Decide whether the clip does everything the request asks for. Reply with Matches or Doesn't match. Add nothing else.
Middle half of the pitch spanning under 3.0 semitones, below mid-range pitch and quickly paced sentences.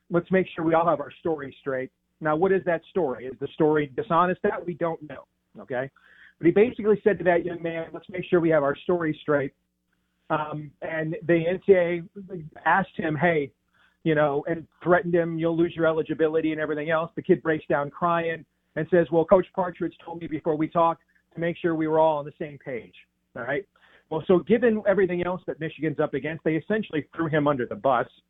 Doesn't match